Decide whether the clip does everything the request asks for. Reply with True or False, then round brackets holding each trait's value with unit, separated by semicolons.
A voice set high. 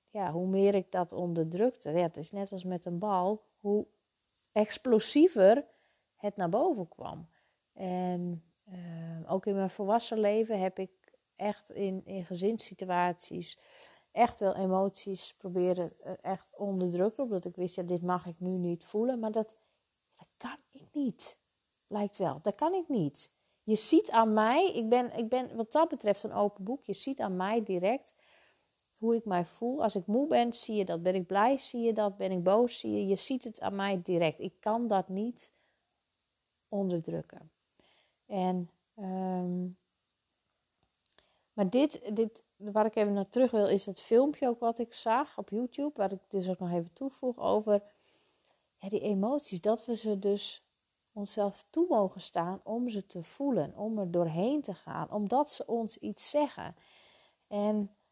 True (205 Hz)